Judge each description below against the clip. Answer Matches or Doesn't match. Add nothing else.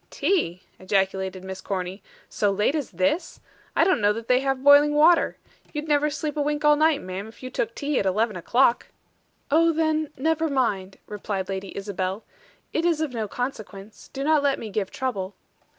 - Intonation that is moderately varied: Doesn't match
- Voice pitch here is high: Matches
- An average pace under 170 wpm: Doesn't match